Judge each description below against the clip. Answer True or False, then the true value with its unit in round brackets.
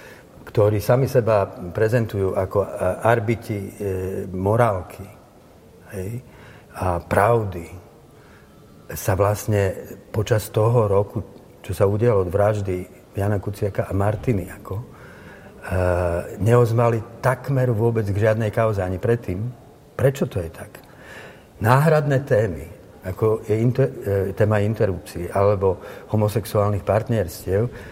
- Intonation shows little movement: False (3.2 semitones)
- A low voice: True (105 Hz)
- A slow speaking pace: True (105 wpm)